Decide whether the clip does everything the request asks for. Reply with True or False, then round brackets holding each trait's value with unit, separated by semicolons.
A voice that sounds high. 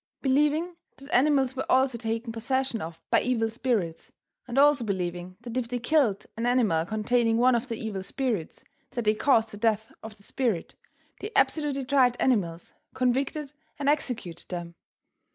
True (240 Hz)